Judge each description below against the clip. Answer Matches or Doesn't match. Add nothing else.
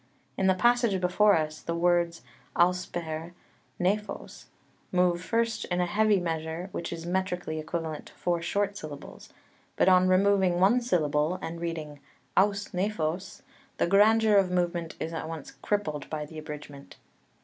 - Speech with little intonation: Doesn't match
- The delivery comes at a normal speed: Matches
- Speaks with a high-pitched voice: Doesn't match